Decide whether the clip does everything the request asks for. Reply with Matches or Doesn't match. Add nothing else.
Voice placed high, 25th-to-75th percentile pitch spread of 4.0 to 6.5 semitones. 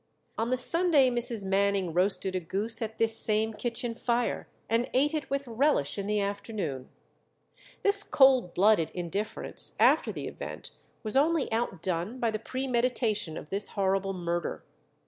Matches